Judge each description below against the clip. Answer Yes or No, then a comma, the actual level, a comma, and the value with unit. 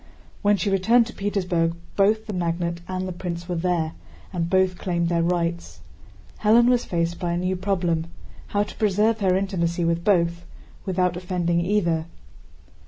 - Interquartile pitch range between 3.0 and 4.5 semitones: No, narrow, 2.5 semitones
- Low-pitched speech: No, medium, 180 Hz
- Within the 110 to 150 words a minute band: No, average, 160 wpm